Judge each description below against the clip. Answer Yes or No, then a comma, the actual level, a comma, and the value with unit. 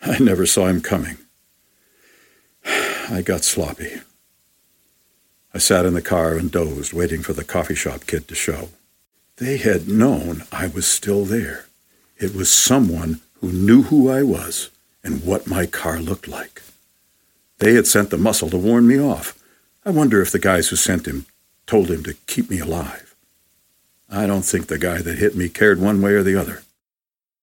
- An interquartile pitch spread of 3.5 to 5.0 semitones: Yes, average, 3.8 semitones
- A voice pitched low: Yes, very low, 95 Hz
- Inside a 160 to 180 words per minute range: Yes, average, 175 wpm